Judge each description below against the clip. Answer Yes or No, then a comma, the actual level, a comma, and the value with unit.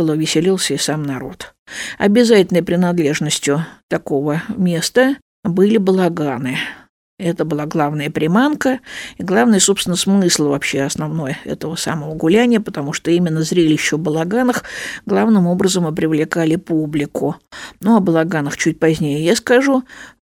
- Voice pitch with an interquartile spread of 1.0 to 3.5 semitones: No, average, 4.4 semitones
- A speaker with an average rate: Yes, average, 120 wpm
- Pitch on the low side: No, medium, 165 Hz